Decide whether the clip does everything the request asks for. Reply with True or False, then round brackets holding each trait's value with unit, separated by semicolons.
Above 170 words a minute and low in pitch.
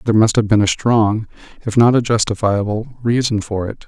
True (200 wpm; 110 Hz)